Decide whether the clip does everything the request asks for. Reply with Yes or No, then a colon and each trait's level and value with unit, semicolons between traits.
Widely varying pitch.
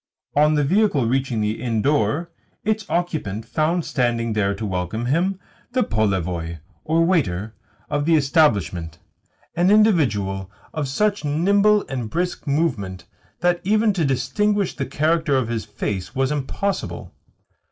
Yes: wide, 8.1 semitones